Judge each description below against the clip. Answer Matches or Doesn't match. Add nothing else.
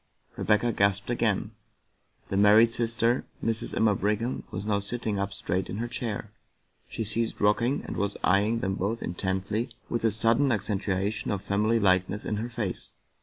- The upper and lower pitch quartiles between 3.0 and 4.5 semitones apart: Doesn't match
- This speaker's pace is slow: Doesn't match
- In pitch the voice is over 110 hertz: Doesn't match